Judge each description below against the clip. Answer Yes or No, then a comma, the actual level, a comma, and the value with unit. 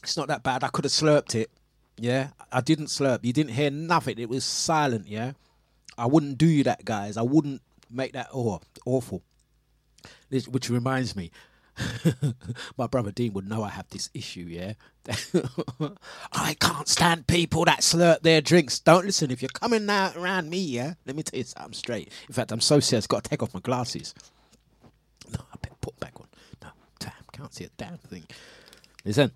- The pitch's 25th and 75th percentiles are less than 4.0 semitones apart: No, average, 4.6 semitones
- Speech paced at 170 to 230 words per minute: Yes, average, 190 wpm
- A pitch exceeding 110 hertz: Yes, low, 135 Hz